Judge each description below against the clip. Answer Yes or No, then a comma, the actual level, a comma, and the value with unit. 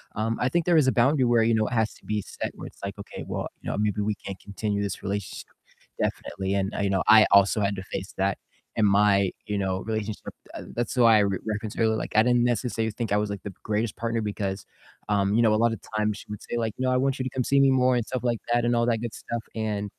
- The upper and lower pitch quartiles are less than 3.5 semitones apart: Yes, average, 2.7 semitones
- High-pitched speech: No, low, 110 Hz